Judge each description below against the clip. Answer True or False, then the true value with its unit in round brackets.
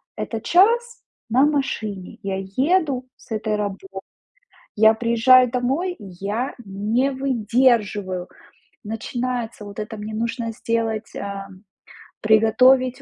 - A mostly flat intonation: False (3.5 semitones)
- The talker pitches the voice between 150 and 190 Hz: False (230 Hz)